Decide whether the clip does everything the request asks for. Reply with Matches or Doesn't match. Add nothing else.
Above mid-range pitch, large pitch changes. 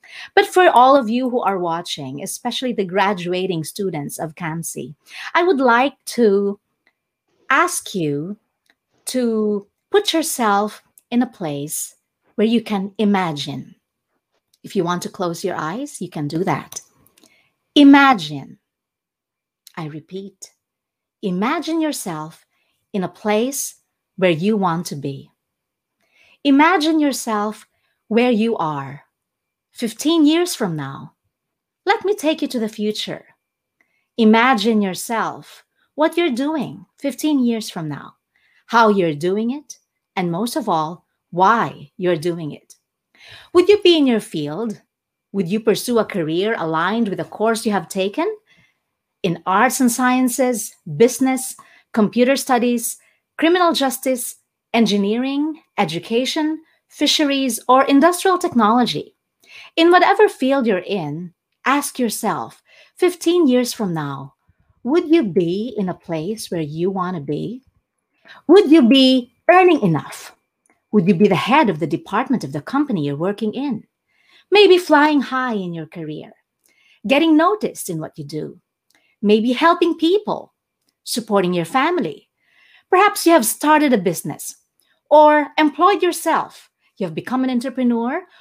Matches